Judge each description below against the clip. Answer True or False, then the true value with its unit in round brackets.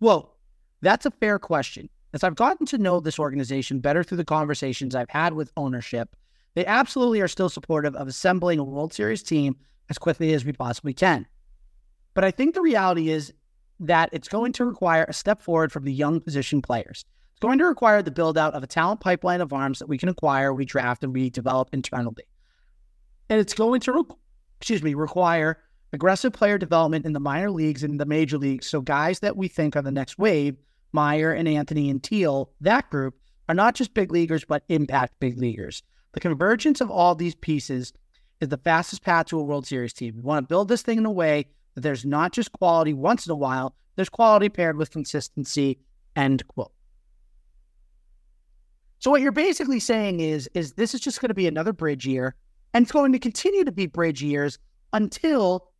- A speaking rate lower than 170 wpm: False (200 wpm)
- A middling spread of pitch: False (6.0 semitones)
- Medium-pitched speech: True (160 Hz)